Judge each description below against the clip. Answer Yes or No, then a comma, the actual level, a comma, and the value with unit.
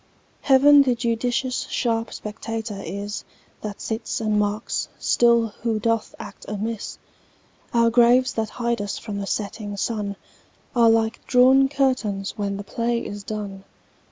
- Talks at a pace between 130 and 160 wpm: Yes, average, 140 wpm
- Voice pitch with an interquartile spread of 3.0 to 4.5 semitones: No, narrow, 2.4 semitones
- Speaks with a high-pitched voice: Yes, high, 225 Hz